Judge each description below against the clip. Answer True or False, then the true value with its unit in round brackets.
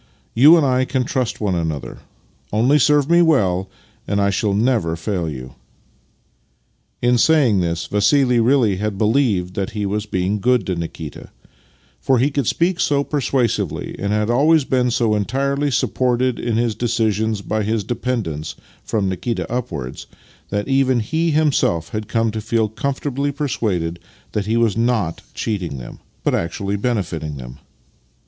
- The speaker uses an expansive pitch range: False (4.9 semitones)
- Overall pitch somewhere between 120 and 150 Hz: False (110 Hz)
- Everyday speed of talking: True (160 wpm)